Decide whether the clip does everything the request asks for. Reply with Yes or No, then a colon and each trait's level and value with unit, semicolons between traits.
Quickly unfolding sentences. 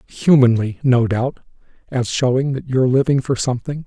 No: average, 155 wpm